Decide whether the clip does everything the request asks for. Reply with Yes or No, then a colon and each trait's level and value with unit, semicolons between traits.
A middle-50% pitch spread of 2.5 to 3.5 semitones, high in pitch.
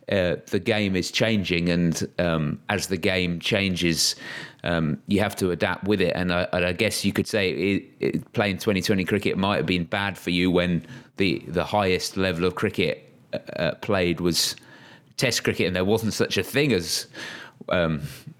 No: average, 2.9 semitones; very low, 90 Hz